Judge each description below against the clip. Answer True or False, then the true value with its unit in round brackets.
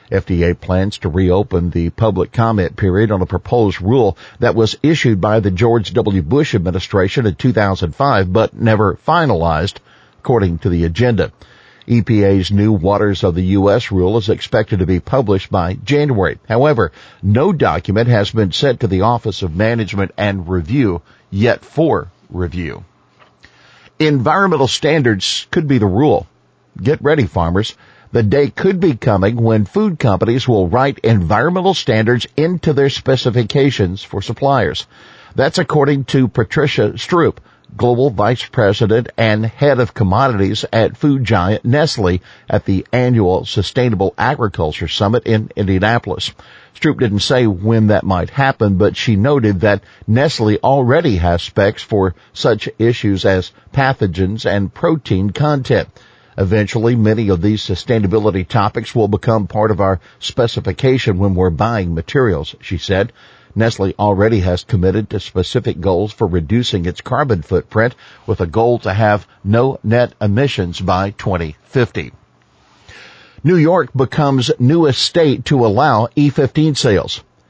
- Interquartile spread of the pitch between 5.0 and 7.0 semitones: False (4.3 semitones)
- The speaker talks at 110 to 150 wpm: True (140 wpm)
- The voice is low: True (110 Hz)